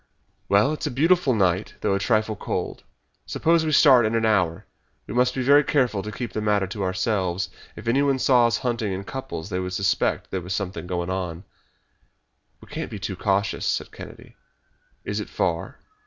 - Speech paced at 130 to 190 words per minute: No, average, 200 wpm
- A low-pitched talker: Yes, low, 105 Hz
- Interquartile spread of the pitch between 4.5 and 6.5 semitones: Yes, average, 5.1 semitones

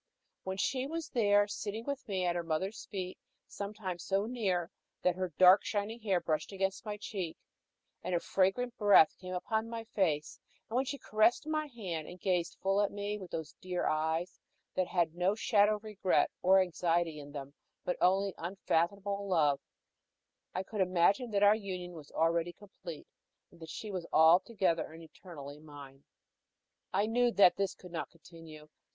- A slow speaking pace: No, average, 170 wpm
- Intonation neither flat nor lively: Yes, average, 3.5 semitones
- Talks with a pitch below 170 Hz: No, medium, 185 Hz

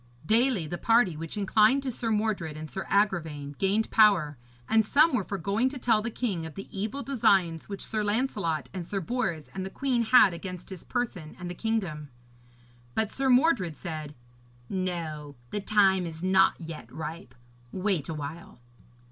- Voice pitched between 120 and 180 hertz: No, high, 190 Hz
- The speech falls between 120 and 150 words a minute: No, average, 175 wpm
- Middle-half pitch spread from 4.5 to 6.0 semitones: Yes, average, 5.2 semitones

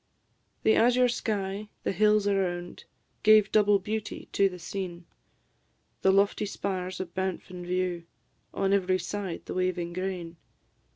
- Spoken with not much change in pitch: Yes, narrow, 2.2 semitones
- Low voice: No, high, 190 Hz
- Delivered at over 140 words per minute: No, slow, 135 wpm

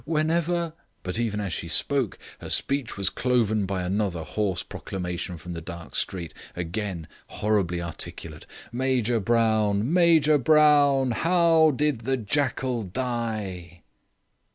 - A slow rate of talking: Yes, slow, 130 wpm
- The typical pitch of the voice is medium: No, low, 110 Hz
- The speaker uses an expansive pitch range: Yes, wide, 7.0 semitones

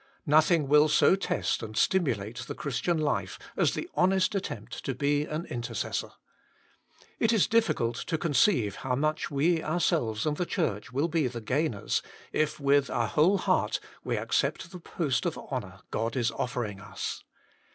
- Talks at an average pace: Yes, average, 160 wpm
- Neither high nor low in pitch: Yes, medium, 145 Hz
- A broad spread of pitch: Yes, wide, 5.9 semitones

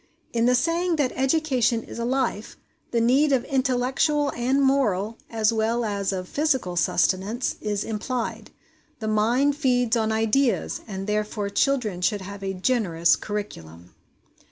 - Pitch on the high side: Yes, high, 230 Hz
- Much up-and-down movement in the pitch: No, average, 4.2 semitones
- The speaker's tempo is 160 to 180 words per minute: No, average, 145 wpm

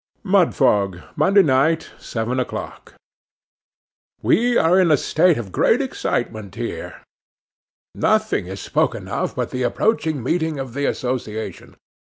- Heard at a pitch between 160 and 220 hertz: No, low, 135 Hz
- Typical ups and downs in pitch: No, wide, 7.3 semitones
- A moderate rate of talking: No, slow, 125 wpm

